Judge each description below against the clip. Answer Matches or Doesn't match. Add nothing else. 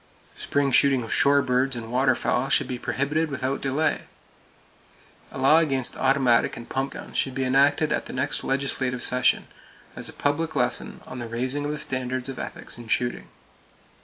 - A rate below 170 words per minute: Doesn't match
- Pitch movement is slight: Matches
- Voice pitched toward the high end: Doesn't match